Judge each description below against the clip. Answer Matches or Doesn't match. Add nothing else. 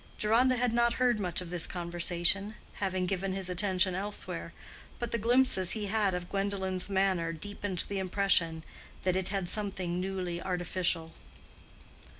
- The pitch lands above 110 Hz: Matches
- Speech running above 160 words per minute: Doesn't match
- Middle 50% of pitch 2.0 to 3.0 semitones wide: Matches